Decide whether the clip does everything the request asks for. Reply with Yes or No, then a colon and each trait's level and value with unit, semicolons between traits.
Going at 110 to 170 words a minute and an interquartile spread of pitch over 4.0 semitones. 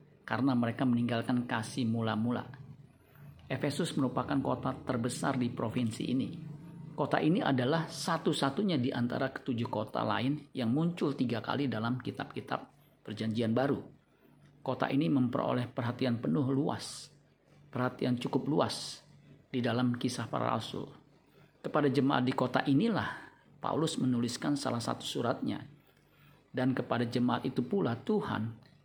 No: average, 125 wpm; average, 2.7 semitones